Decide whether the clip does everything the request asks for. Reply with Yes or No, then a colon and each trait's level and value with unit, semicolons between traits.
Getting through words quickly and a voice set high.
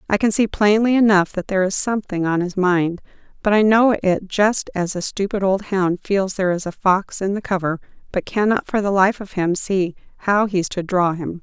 Yes: fast, 225 wpm; high, 195 Hz